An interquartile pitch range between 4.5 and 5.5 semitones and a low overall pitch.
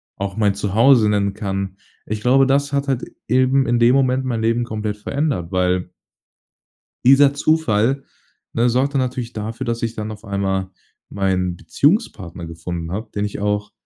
Yes: average, 4.8 semitones; low, 110 Hz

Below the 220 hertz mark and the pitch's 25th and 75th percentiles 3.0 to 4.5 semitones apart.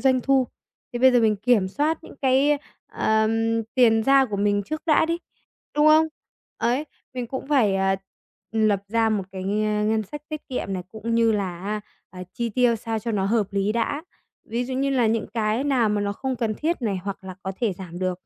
No: high, 225 Hz; average, 4.2 semitones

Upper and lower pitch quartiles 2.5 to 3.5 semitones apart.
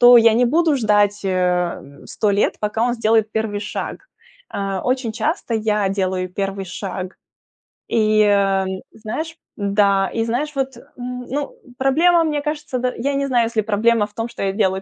No: average, 4.0 semitones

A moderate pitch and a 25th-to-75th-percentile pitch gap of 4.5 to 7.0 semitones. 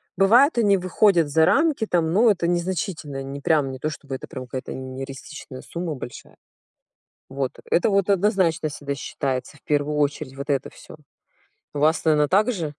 Yes: medium, 155 Hz; average, 5.2 semitones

